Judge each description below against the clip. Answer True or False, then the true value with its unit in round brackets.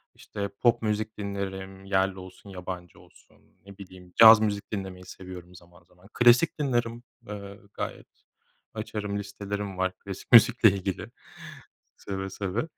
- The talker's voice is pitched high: False (100 Hz)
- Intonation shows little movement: True (2.3 semitones)